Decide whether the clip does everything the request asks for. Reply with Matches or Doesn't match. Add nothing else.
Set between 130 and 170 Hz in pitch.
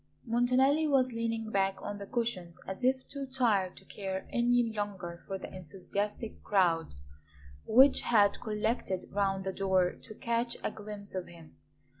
Doesn't match